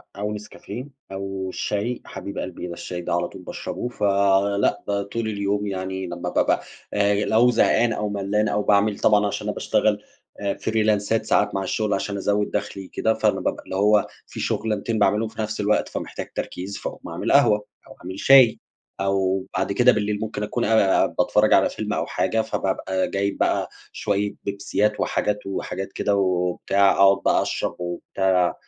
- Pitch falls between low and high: No, low, 100 Hz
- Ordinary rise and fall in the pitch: No, narrow, 1.6 semitones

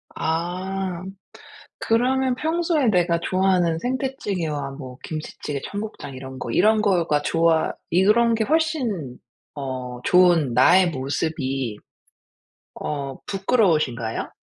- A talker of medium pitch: Yes, medium, 175 Hz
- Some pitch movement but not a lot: No, wide, 7.2 semitones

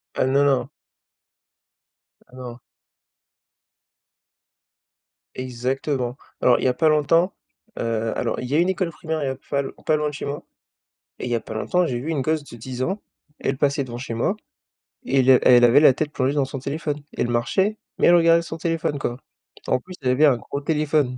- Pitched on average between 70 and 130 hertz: No, medium, 140 Hz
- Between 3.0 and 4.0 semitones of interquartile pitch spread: Yes, average, 3.7 semitones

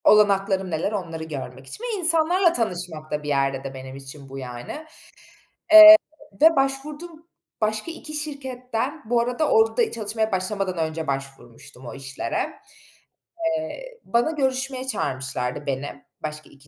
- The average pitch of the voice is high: Yes, high, 195 Hz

